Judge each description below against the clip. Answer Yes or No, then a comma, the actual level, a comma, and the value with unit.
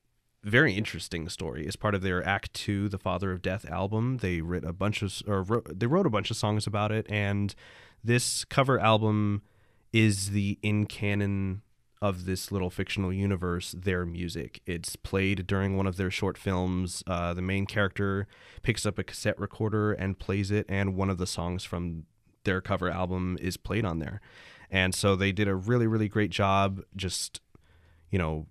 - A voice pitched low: Yes, low, 100 Hz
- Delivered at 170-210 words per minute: Yes, average, 185 wpm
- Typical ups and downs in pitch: No, narrow, 2.3 semitones